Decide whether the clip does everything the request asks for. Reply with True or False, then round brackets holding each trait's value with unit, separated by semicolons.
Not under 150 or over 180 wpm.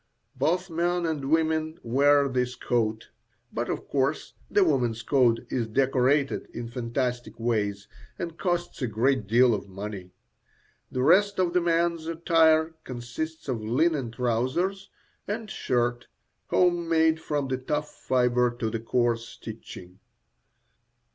False (135 wpm)